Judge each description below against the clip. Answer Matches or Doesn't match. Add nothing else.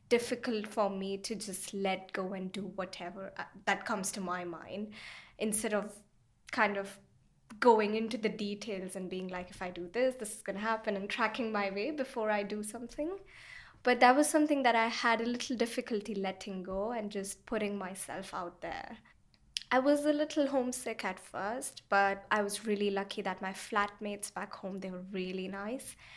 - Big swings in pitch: Doesn't match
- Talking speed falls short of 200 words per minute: Matches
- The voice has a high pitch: Matches